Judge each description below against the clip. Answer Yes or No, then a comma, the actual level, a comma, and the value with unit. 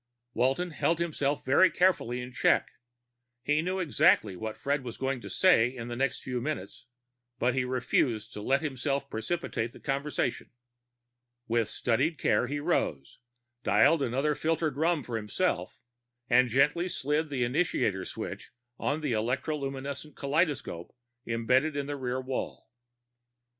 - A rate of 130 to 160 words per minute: Yes, average, 140 wpm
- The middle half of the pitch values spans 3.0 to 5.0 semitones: Yes, average, 3.9 semitones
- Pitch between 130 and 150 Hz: Yes, low, 135 Hz